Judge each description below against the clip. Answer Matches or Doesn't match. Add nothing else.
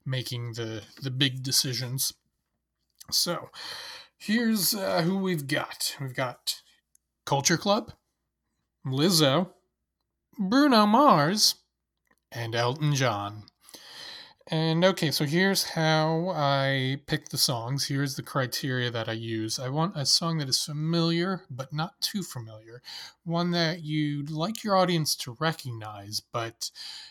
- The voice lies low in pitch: Doesn't match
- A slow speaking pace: Matches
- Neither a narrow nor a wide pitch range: Doesn't match